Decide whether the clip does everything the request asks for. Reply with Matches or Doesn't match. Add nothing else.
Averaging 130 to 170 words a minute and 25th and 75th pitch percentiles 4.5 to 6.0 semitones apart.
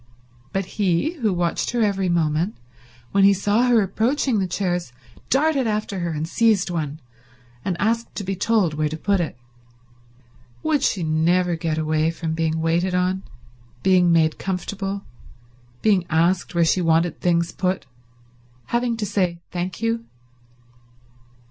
Doesn't match